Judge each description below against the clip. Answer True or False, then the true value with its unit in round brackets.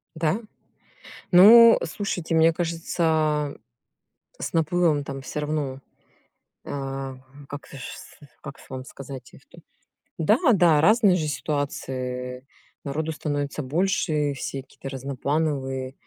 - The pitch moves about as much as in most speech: True (3.3 semitones)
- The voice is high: False (150 Hz)